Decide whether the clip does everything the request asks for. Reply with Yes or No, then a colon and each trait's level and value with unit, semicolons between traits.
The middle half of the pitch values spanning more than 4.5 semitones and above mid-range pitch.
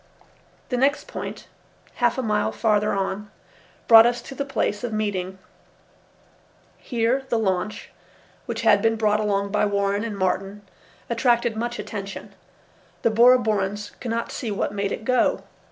No: average, 2.8 semitones; high, 215 Hz